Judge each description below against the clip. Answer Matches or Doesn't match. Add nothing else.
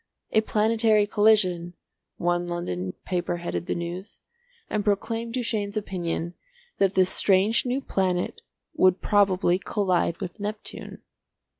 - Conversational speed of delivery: Doesn't match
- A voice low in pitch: Doesn't match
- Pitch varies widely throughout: Doesn't match